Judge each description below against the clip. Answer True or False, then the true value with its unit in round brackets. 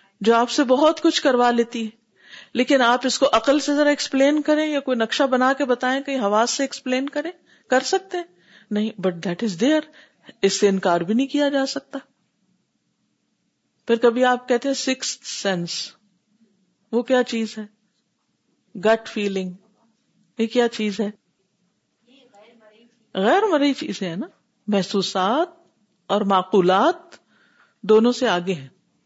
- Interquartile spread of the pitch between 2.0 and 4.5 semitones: False (4.9 semitones)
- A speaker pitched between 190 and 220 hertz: False (235 Hz)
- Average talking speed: True (150 wpm)